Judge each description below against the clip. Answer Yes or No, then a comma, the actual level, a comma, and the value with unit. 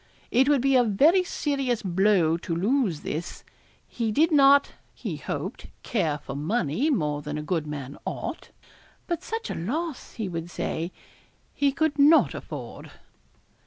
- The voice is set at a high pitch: Yes, high, 220 Hz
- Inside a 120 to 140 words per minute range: No, average, 155 wpm